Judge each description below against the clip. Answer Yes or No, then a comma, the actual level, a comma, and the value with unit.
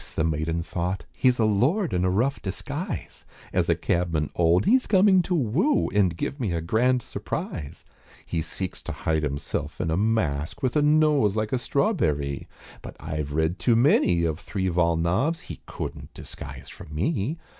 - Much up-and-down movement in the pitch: Yes, wide, 8.1 semitones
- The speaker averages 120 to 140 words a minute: No, average, 175 wpm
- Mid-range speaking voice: No, very low, 95 Hz